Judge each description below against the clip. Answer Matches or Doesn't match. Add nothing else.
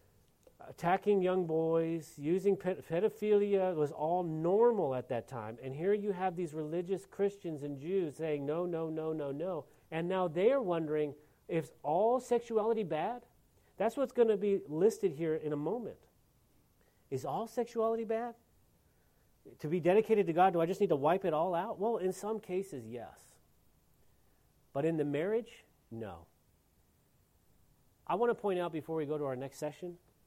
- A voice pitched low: Doesn't match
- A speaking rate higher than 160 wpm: Matches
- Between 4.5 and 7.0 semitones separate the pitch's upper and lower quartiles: Matches